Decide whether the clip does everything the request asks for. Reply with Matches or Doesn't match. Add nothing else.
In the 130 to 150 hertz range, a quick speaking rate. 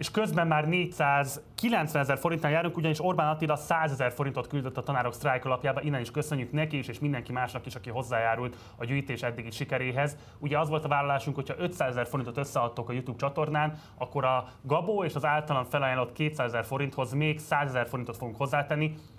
Matches